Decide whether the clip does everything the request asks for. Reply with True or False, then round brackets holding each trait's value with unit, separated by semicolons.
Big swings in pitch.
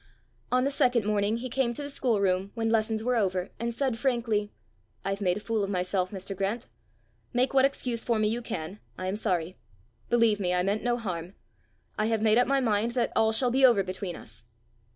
False (3.6 semitones)